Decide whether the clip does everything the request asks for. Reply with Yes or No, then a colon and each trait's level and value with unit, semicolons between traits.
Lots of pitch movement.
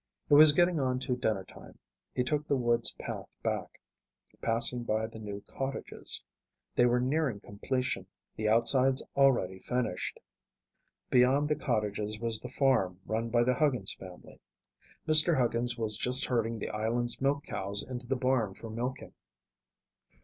No: average, 3.4 semitones